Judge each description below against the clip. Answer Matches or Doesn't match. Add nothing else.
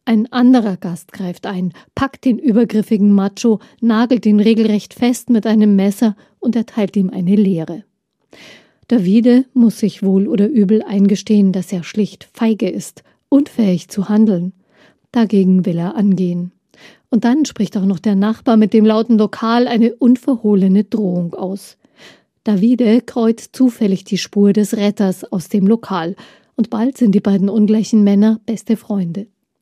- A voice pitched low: Doesn't match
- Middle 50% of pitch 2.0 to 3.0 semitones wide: Matches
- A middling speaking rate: Matches